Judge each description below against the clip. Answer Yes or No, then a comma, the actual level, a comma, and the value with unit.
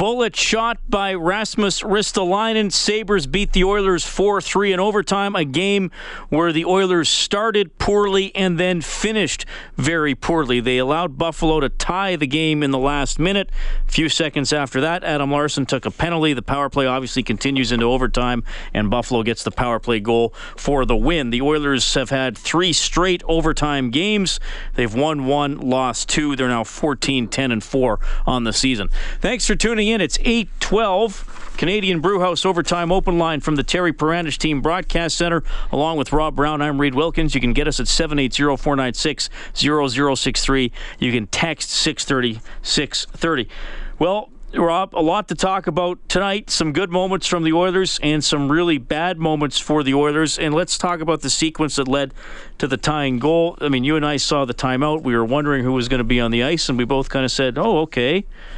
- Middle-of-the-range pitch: Yes, medium, 155 Hz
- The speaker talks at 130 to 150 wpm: No, average, 185 wpm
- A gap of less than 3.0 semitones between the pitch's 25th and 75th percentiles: No, average, 5.2 semitones